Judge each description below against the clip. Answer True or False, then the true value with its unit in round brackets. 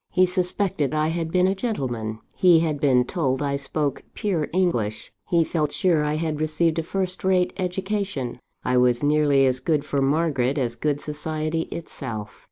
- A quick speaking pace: False (175 wpm)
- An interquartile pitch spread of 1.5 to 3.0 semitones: False (4.4 semitones)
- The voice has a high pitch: False (155 Hz)